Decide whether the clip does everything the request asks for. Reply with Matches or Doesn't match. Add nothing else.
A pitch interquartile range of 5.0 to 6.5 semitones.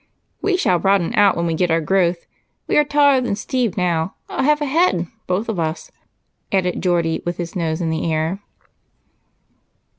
Matches